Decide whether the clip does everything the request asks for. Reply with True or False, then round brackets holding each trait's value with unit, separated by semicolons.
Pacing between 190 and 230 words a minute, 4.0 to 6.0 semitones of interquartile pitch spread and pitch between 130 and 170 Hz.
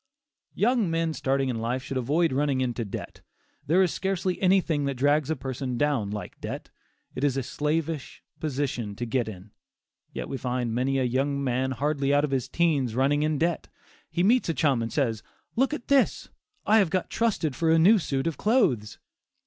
True (195 wpm; 4.4 semitones; 140 Hz)